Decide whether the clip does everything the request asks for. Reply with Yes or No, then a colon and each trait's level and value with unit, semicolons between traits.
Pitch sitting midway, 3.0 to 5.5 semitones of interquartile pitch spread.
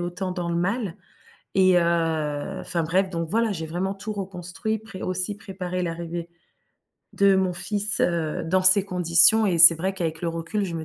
No: medium, 180 Hz; narrow, 2.4 semitones